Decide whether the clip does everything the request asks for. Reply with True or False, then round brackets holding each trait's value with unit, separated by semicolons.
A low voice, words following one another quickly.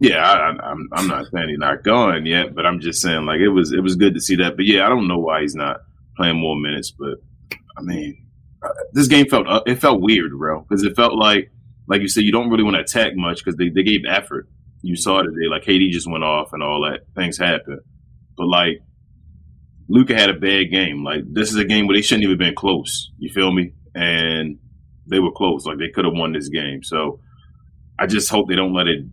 True (90 Hz; 240 wpm)